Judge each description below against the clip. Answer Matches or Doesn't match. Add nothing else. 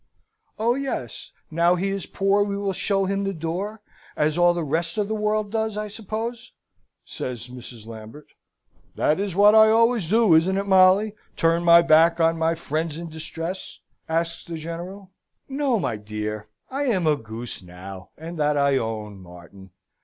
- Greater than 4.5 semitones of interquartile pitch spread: Matches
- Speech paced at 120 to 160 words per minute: Doesn't match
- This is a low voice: Doesn't match